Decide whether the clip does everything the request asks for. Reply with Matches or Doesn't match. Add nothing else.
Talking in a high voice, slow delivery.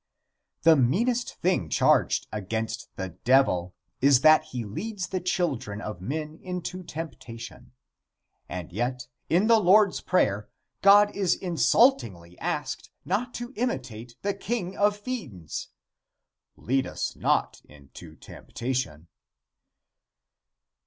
Doesn't match